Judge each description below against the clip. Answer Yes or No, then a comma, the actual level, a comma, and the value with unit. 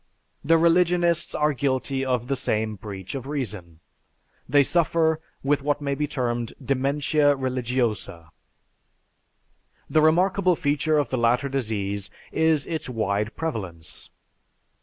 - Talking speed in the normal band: No, slow, 120 wpm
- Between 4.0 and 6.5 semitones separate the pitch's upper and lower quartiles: Yes, wide, 5.4 semitones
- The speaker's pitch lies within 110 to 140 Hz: Yes, low, 135 Hz